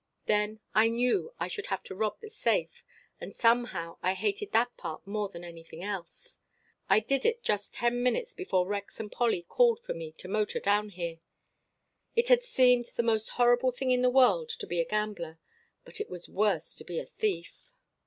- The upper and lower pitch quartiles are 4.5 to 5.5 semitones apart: Yes, average, 5.1 semitones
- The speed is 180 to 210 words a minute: Yes, average, 195 wpm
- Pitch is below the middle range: No, high, 220 Hz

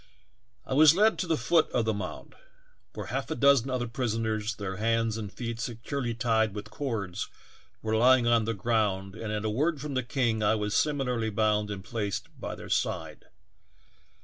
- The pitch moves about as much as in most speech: Yes, average, 3.0 semitones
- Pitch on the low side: Yes, low, 115 Hz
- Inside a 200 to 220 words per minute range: No, average, 190 wpm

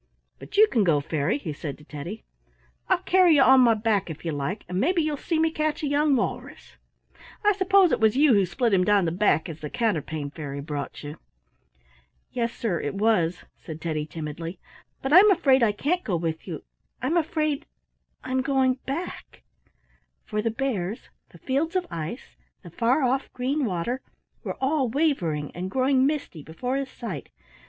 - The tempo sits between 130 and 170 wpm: No, average, 185 wpm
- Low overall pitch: No, high, 230 Hz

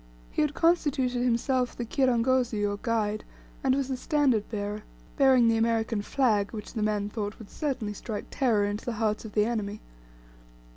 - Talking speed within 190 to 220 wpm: No, average, 175 wpm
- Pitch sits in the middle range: No, high, 230 Hz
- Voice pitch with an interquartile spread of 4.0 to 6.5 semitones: No, average, 3.6 semitones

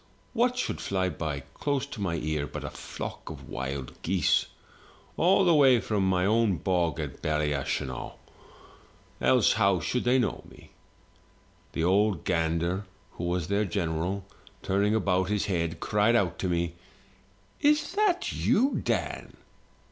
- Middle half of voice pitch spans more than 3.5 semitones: Yes, wide, 5.5 semitones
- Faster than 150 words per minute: No, average, 145 wpm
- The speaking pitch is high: No, very low, 95 Hz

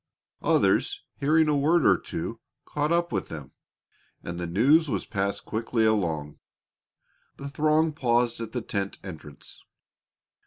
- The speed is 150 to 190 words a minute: No, average, 140 wpm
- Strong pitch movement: Yes, wide, 7.6 semitones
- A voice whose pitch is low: Yes, low, 120 Hz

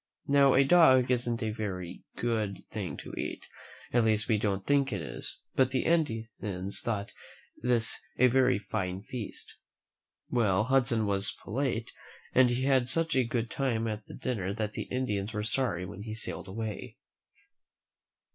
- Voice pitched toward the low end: Yes, low, 115 Hz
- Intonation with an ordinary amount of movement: Yes, average, 3.7 semitones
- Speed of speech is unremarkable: Yes, average, 160 wpm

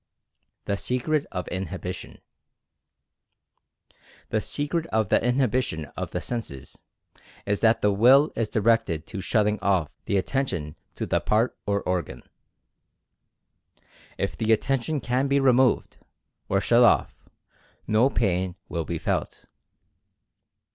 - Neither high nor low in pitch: No, low, 110 Hz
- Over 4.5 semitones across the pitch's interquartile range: Yes, average, 4.9 semitones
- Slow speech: Yes, slow, 120 wpm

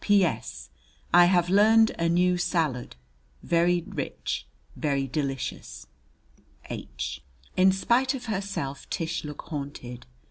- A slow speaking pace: Yes, slow, 110 wpm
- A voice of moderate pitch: Yes, medium, 170 Hz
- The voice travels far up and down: Yes, wide, 5.7 semitones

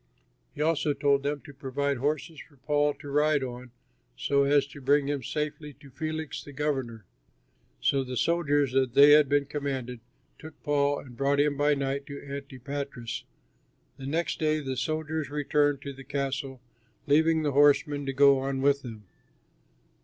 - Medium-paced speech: Yes, average, 170 wpm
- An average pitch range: No, narrow, 1.5 semitones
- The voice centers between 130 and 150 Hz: Yes, medium, 140 Hz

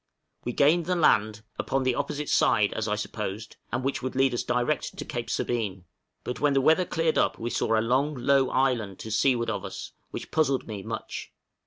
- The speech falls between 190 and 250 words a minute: Yes, fast, 205 wpm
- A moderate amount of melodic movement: Yes, average, 4.1 semitones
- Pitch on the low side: Yes, low, 125 Hz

